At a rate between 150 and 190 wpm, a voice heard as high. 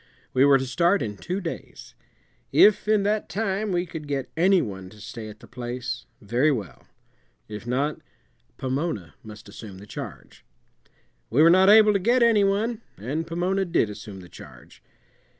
No: average, 170 wpm; medium, 150 Hz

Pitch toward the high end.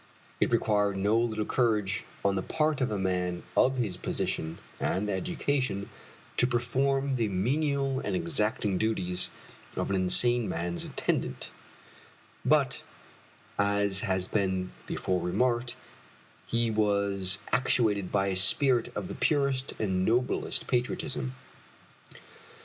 No: low, 105 Hz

